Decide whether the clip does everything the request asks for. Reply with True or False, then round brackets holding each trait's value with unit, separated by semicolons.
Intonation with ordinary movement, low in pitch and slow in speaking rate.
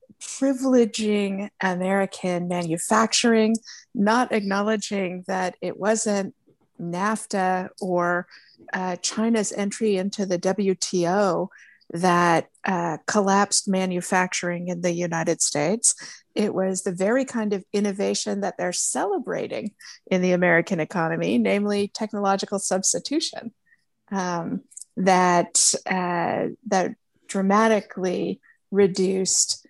False (3.0 semitones; 195 Hz; 95 wpm)